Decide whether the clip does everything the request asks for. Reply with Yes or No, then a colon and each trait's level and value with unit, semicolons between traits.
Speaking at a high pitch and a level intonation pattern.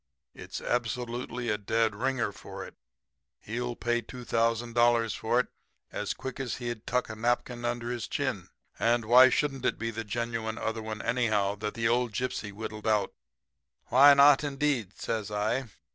No: low, 120 Hz; narrow, 1.9 semitones